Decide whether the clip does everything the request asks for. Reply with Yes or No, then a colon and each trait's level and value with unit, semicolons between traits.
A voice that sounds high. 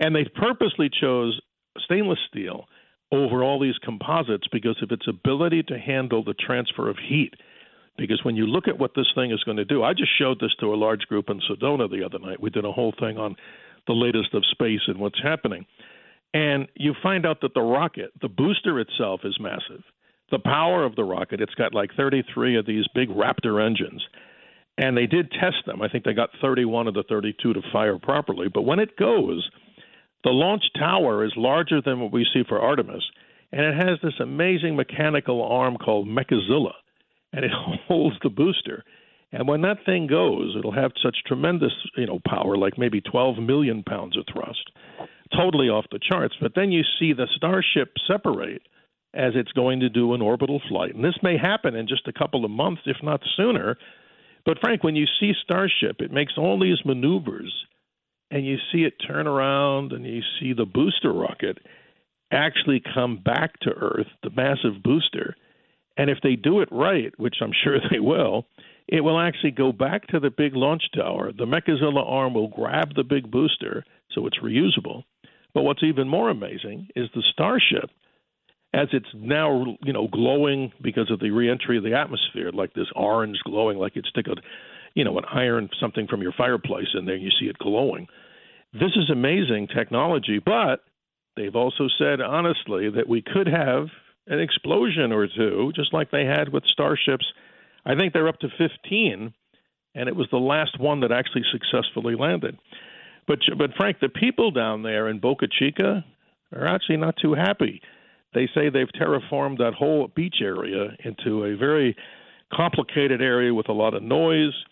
No: low, 135 Hz